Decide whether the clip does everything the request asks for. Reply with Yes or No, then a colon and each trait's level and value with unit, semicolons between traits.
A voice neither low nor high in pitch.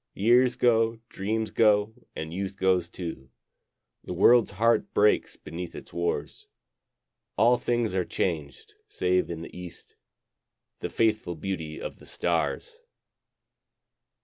No: low, 100 Hz